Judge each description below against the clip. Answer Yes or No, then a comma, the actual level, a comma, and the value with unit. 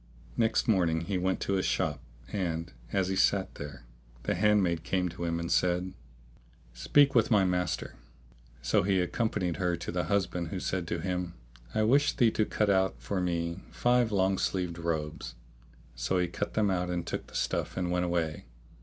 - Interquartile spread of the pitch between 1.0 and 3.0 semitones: Yes, narrow, 2.6 semitones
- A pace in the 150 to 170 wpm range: No, average, 185 wpm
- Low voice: Yes, very low, 90 Hz